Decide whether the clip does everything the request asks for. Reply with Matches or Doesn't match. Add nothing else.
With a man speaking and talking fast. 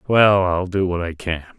Matches